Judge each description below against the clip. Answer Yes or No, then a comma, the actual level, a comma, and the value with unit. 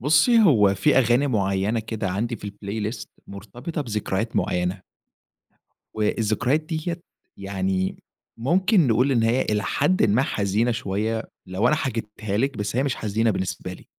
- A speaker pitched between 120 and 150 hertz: No, low, 110 Hz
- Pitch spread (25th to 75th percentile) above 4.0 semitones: Yes, average, 4.7 semitones